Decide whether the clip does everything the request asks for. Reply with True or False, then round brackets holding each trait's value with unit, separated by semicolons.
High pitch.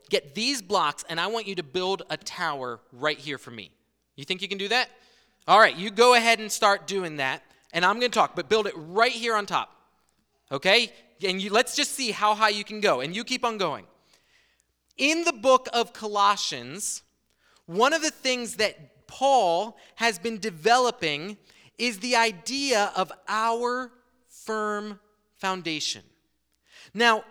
True (215 Hz)